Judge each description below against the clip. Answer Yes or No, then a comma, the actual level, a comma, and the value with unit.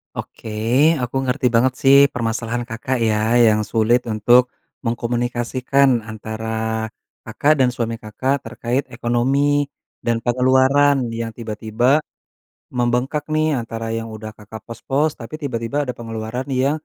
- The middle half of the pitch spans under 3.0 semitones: Yes, narrow, 2.6 semitones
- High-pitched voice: No, low, 120 Hz